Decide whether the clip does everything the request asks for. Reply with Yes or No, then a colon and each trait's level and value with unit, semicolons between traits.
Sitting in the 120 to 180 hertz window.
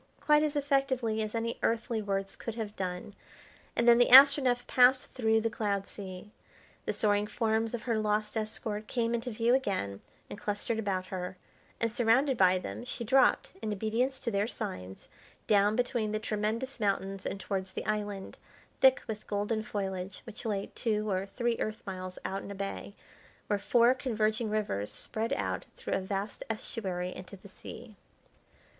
No: high, 215 Hz